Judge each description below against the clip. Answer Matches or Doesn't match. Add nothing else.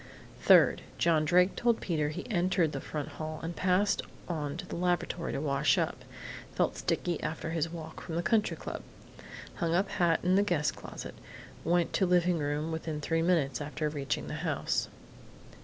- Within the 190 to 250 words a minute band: Doesn't match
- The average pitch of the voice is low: Doesn't match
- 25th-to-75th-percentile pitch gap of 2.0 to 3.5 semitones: Matches